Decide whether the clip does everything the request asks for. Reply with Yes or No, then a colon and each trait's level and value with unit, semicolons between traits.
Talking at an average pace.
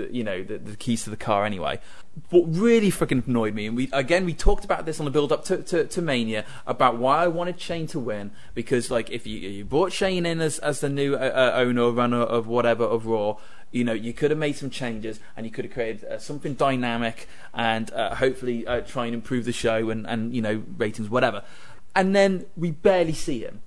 No: fast, 235 wpm